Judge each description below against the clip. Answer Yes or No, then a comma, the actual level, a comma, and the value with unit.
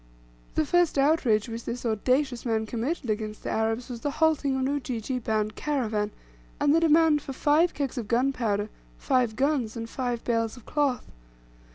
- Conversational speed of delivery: Yes, average, 175 wpm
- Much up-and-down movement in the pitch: No, average, 4.4 semitones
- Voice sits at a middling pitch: No, very high, 250 Hz